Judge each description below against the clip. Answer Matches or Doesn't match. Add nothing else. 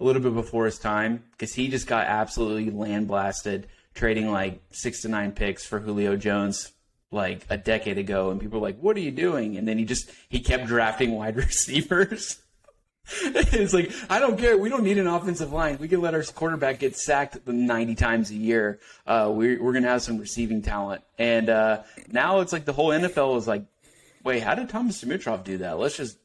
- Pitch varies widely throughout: Matches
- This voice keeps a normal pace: Doesn't match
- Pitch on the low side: Matches